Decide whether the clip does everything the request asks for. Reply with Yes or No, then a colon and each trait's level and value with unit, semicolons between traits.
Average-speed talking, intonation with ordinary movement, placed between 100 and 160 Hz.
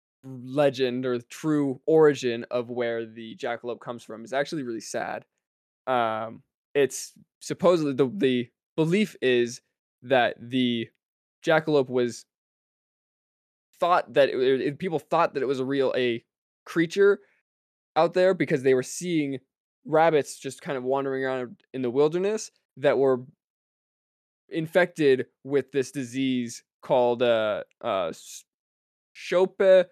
No: slow, 130 wpm; average, 4.4 semitones; low, 135 Hz